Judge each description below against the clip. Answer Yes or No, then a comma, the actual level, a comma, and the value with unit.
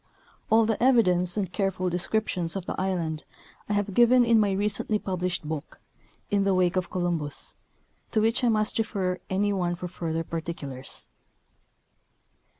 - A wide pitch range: No, average, 3.3 semitones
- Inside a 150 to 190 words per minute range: Yes, average, 160 wpm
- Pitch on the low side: No, medium, 185 Hz